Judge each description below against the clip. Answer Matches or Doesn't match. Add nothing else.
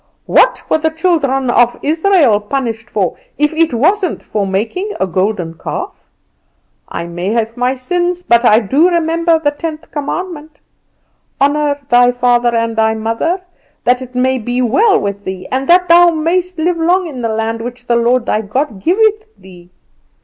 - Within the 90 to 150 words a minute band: Doesn't match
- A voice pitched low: Doesn't match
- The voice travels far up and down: Matches